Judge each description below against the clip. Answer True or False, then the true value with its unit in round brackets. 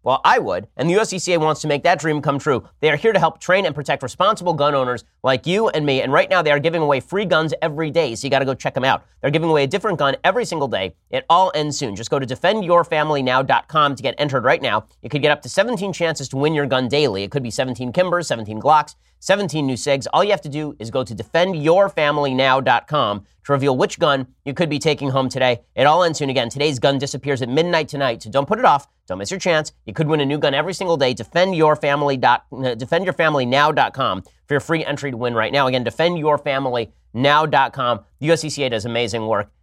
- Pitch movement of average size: True (3.8 semitones)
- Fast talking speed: True (240 wpm)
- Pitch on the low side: False (145 Hz)